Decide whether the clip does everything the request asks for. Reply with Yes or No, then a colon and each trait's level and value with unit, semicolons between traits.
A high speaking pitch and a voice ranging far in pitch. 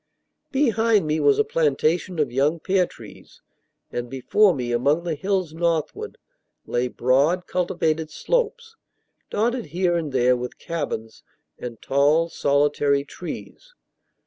No: medium, 160 Hz; wide, 5.8 semitones